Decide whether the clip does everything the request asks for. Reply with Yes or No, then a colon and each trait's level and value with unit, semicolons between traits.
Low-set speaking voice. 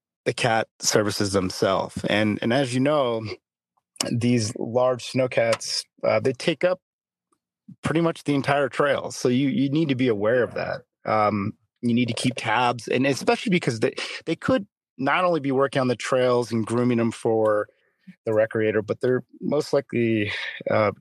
Yes: low, 125 Hz